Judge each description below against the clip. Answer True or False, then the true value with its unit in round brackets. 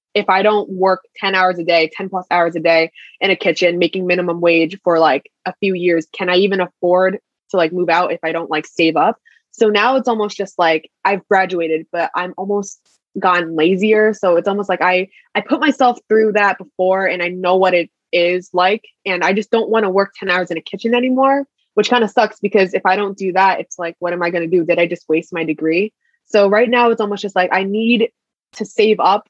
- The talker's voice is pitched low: False (190 Hz)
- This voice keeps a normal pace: False (240 wpm)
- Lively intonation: False (3.2 semitones)